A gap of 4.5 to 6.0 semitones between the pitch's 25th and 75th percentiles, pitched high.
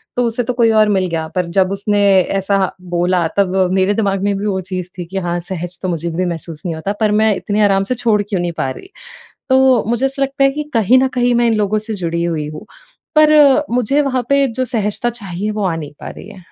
Yes: average, 5.0 semitones; high, 205 Hz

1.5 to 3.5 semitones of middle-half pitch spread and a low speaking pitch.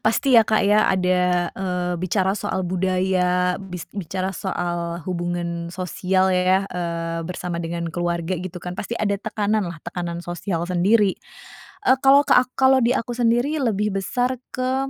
No: average, 3.2 semitones; medium, 185 Hz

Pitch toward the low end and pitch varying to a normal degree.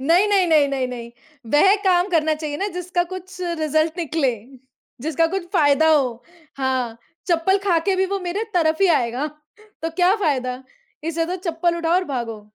No: very high, 325 Hz; average, 4.3 semitones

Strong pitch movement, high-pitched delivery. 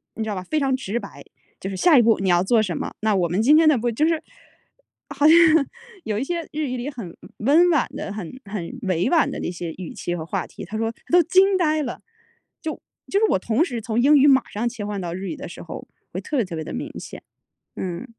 Yes: wide, 7.4 semitones; high, 230 Hz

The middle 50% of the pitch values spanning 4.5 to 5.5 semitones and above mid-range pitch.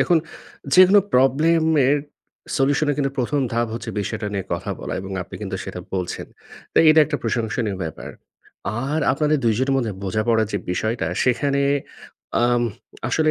No: average, 5.0 semitones; low, 125 Hz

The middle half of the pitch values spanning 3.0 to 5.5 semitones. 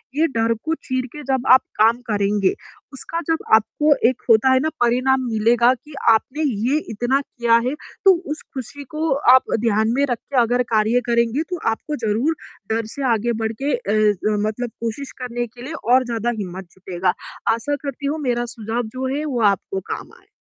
Yes: average, 3.6 semitones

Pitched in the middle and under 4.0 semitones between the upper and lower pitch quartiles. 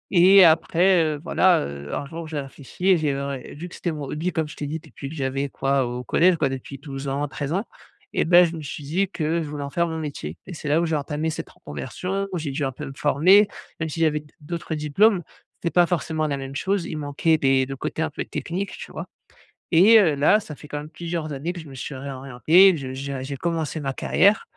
Yes: medium, 155 Hz; average, 3.6 semitones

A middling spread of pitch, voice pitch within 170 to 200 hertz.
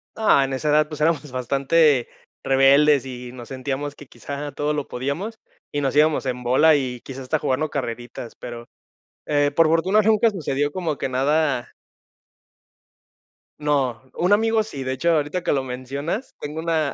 No: average, 3.2 semitones; medium, 145 Hz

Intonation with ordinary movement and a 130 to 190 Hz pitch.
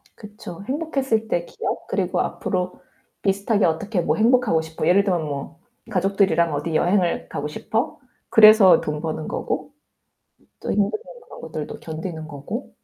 Yes: average, 4.9 semitones; medium, 185 Hz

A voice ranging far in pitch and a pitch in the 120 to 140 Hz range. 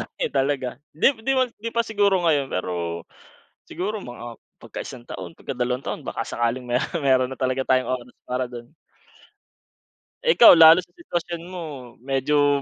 Yes: wide, 6.1 semitones; low, 135 Hz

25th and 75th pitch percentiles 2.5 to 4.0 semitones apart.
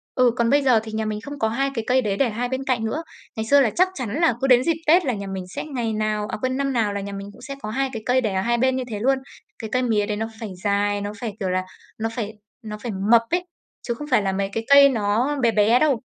Yes: average, 3.6 semitones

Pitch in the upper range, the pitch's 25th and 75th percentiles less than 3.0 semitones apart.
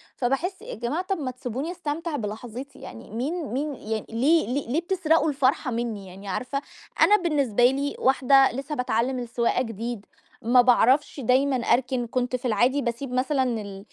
No: very high, 255 Hz; average, 3.3 semitones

